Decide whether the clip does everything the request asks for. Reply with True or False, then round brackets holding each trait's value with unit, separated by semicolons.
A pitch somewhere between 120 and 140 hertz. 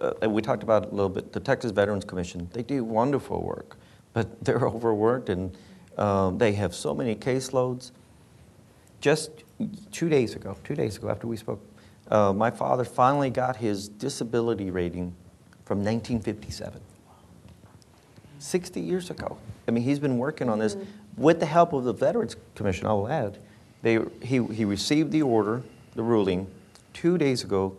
False (110 Hz)